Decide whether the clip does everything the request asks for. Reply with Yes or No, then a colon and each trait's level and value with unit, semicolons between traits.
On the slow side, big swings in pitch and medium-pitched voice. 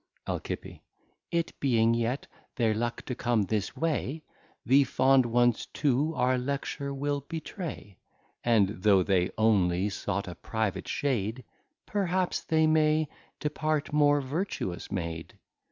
No: slow, 125 wpm; wide, 5.7 semitones; low, 130 Hz